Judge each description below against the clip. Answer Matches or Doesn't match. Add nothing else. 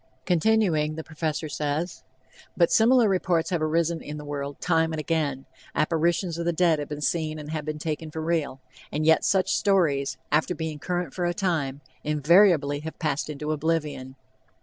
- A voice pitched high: Doesn't match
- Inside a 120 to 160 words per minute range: Doesn't match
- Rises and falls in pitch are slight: Matches